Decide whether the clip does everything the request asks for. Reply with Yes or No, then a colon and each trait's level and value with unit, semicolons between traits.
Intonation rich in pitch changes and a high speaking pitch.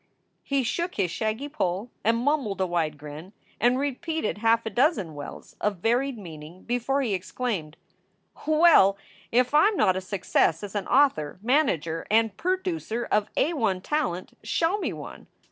Yes: wide, 7.1 semitones; high, 225 Hz